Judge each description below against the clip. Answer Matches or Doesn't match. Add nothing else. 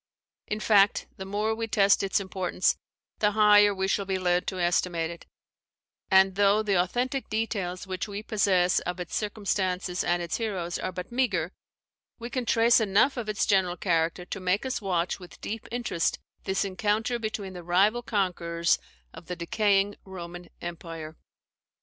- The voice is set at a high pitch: Matches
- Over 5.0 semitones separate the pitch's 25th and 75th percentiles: Doesn't match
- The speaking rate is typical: Matches